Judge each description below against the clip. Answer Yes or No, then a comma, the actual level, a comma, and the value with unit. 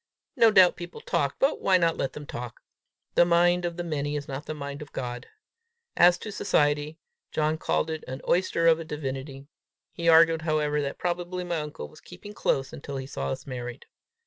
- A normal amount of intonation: Yes, average, 3.6 semitones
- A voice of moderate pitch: Yes, medium, 155 Hz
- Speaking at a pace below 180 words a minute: No, average, 200 wpm